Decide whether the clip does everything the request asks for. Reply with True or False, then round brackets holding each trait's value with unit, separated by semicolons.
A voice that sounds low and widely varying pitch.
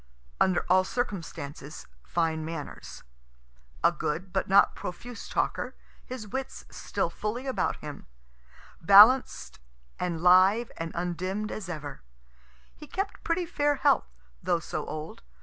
False (185 Hz; 6.6 semitones)